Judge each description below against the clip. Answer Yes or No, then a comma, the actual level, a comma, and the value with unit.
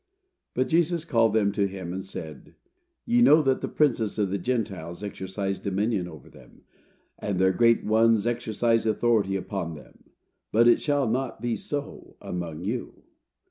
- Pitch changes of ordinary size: Yes, average, 4.0 semitones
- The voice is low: Yes, low, 110 Hz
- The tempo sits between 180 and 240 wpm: No, average, 160 wpm